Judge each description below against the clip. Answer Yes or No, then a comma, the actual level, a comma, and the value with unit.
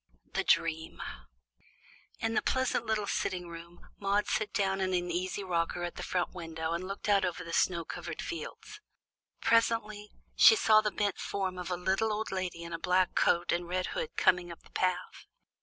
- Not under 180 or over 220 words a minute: Yes, average, 190 wpm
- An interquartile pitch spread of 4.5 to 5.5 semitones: No, average, 3.1 semitones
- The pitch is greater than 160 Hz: Yes, medium, 185 Hz